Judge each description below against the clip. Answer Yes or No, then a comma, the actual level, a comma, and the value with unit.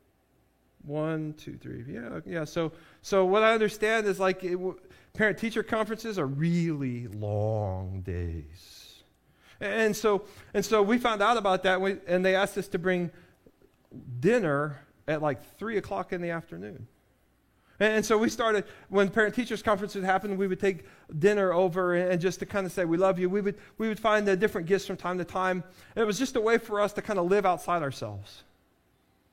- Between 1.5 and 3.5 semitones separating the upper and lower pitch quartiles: No, average, 3.9 semitones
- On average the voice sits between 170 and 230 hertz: Yes, high, 190 Hz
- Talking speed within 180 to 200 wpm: Yes, average, 195 wpm